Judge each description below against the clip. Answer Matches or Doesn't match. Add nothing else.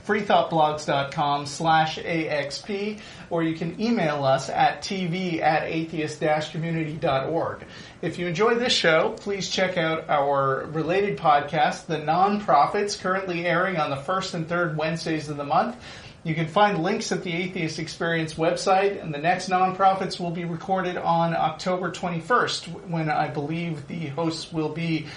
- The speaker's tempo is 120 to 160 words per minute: Matches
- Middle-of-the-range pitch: Matches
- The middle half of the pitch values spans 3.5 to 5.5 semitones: Doesn't match